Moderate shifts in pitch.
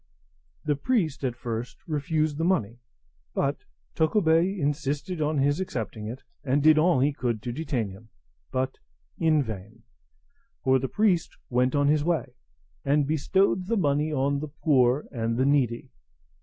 Yes: average, 3.8 semitones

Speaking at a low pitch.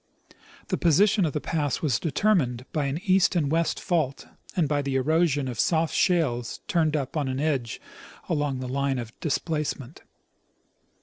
No: medium, 150 Hz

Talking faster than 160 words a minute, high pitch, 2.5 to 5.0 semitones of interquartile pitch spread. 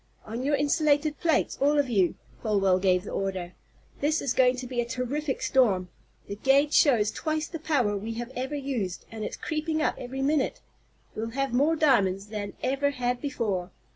No: average, 185 wpm; very high, 255 Hz; wide, 5.5 semitones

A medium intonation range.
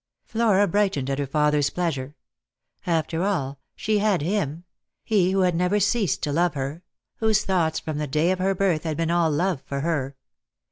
Yes: average, 4.5 semitones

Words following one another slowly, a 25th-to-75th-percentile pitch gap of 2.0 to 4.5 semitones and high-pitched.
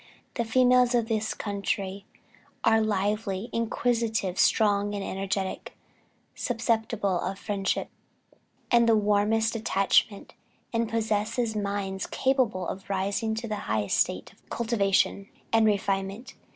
Yes: slow, 115 wpm; narrow, 2.5 semitones; high, 210 Hz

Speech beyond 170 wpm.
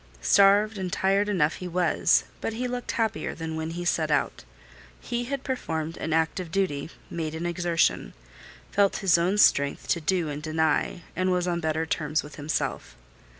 Yes: average, 180 wpm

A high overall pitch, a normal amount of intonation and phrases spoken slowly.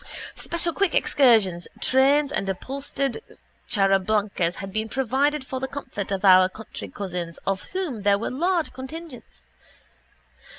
No: high, 235 Hz; wide, 6.3 semitones; slow, 130 wpm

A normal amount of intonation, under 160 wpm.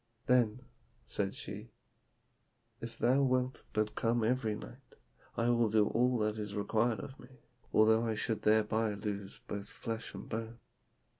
No: narrow, 2.1 semitones; average, 150 wpm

